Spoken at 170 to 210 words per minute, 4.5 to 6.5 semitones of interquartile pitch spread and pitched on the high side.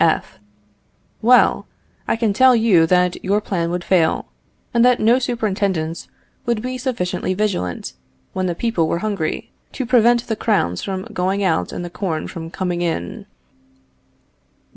No: average, 150 wpm; average, 5.0 semitones; high, 195 Hz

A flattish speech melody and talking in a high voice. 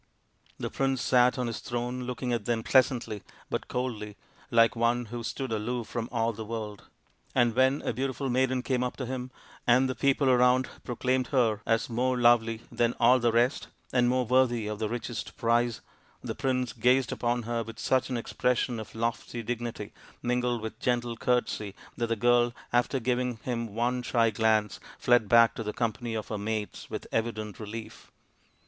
No: narrow, 1.8 semitones; low, 120 Hz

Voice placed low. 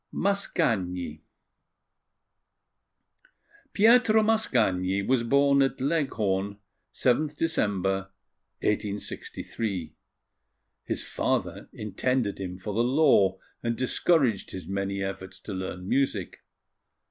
Yes: low, 105 Hz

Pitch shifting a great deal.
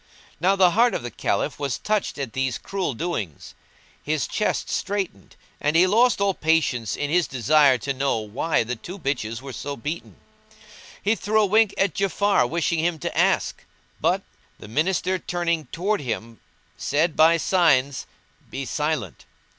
Yes: wide, 6.0 semitones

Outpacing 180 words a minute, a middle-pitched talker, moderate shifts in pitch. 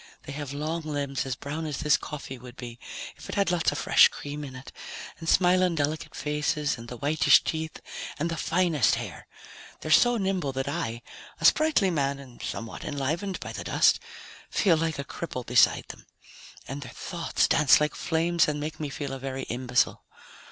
Yes: average, 190 wpm; medium, 150 Hz; average, 3.3 semitones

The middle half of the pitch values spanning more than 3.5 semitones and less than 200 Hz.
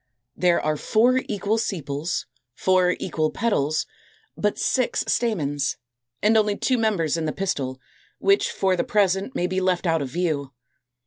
Yes: average, 5.3 semitones; medium, 185 Hz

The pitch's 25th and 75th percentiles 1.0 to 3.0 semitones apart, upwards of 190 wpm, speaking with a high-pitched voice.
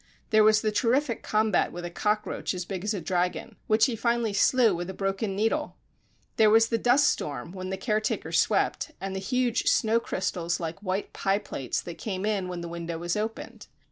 No: average, 3.5 semitones; fast, 205 wpm; high, 205 Hz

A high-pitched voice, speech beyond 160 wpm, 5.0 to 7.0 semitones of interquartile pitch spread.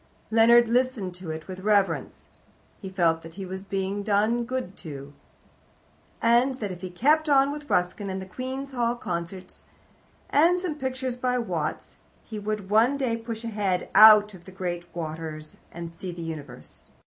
Yes: high, 205 Hz; average, 170 wpm; average, 5.3 semitones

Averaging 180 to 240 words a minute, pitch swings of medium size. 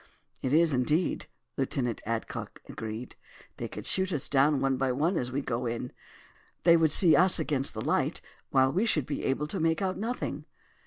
Yes: average, 190 wpm; average, 4.7 semitones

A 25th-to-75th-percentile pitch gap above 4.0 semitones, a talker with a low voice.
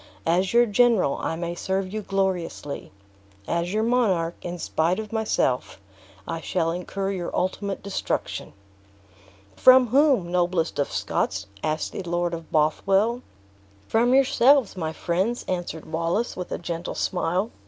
No: average, 4.4 semitones; medium, 185 Hz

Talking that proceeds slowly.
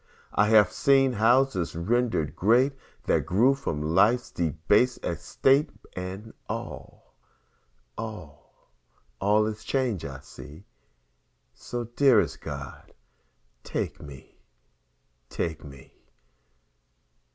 Yes: slow, 95 wpm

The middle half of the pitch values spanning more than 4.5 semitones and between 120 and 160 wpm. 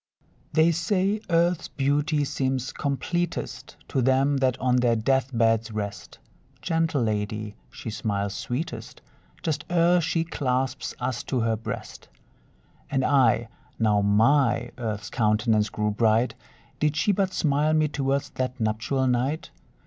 Yes: average, 5.0 semitones; slow, 135 wpm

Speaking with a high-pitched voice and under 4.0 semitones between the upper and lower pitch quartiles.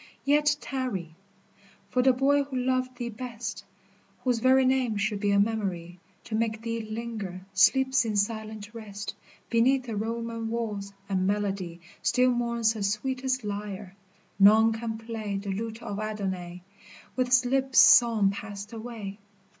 Yes: high, 225 Hz; average, 3.5 semitones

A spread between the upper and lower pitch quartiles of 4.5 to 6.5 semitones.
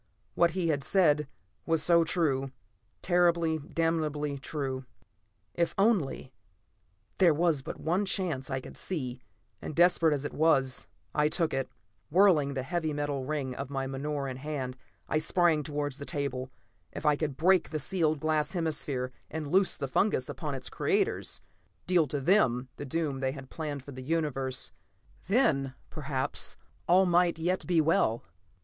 No: average, 3.7 semitones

